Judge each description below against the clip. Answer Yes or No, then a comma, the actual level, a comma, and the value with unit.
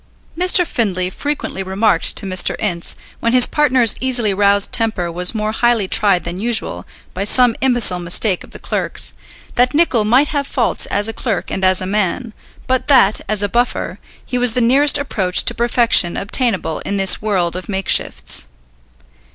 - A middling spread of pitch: Yes, average, 4.5 semitones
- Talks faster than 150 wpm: Yes, average, 175 wpm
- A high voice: Yes, high, 215 Hz